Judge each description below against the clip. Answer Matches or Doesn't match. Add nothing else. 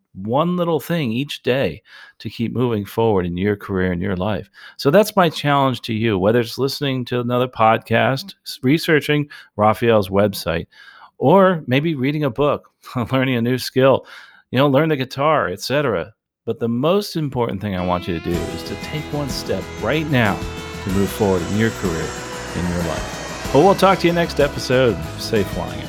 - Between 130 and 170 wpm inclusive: Doesn't match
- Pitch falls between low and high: Doesn't match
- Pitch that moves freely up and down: Matches